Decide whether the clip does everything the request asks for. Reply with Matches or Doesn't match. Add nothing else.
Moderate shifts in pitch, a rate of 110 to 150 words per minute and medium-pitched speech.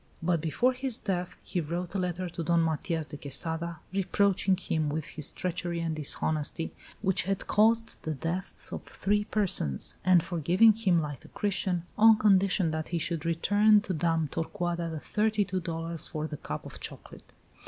Doesn't match